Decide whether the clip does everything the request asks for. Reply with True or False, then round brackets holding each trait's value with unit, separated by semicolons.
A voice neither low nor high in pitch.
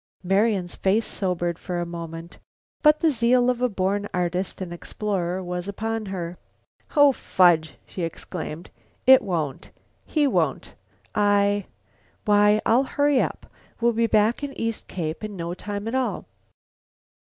False (200 Hz)